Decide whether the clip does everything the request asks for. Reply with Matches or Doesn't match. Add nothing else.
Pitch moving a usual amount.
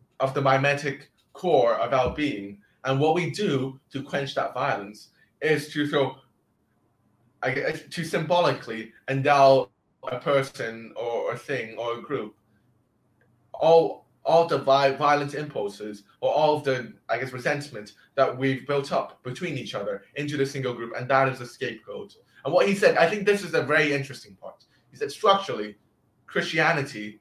Matches